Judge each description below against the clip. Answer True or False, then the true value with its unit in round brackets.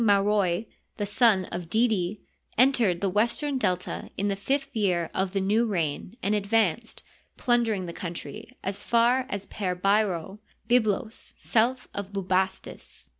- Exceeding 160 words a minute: False (140 wpm)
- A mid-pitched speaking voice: False (205 Hz)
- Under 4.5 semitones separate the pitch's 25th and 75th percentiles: True (3.4 semitones)